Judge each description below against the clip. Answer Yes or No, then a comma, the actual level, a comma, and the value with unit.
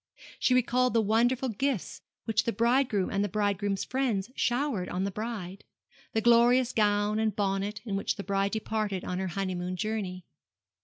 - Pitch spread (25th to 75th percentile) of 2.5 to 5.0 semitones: Yes, average, 3.2 semitones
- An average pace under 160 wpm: No, average, 165 wpm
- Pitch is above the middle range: Yes, high, 210 Hz